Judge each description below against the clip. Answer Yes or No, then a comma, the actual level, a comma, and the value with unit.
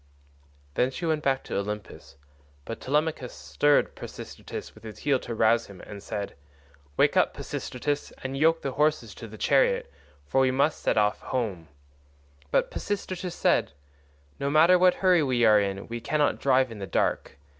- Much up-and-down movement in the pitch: Yes, wide, 6.3 semitones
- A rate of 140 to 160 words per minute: No, average, 170 wpm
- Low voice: Yes, low, 125 Hz